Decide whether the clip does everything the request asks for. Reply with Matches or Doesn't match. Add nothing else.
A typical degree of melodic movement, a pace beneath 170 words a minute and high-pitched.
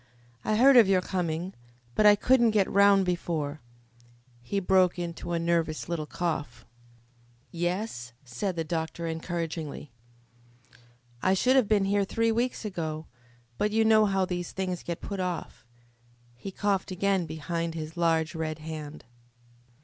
Doesn't match